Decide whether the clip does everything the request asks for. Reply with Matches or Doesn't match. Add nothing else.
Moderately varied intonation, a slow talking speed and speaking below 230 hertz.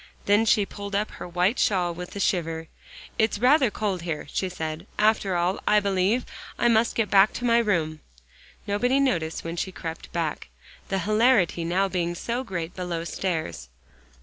Doesn't match